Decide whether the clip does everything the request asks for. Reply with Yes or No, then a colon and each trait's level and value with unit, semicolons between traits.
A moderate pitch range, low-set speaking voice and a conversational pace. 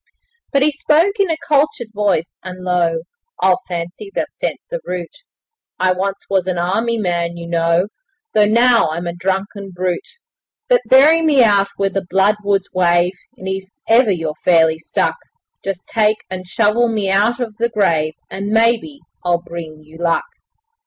No: average, 4.8 semitones; high, 195 Hz; average, 165 wpm